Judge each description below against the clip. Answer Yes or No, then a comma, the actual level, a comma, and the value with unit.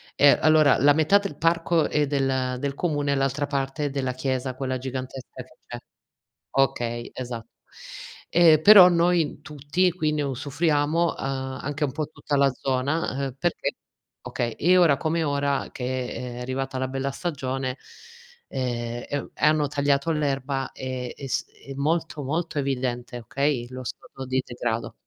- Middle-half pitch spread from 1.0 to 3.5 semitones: Yes, average, 2.7 semitones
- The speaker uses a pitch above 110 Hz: Yes, medium, 140 Hz